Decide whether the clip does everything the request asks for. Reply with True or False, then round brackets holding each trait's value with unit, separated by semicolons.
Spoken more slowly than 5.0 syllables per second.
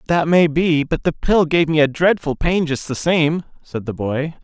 True (4.4 syllables/s)